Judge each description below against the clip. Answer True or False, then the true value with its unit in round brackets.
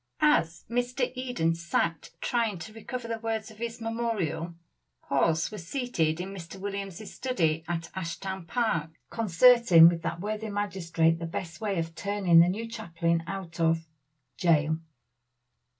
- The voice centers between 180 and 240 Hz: True (185 Hz)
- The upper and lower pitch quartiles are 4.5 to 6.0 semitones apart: True (5.2 semitones)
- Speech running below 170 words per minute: True (145 wpm)